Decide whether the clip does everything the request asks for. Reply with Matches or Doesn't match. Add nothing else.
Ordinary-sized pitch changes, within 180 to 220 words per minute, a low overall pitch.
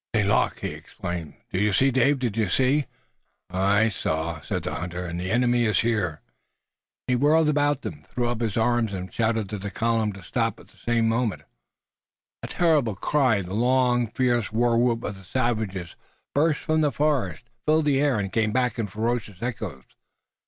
Matches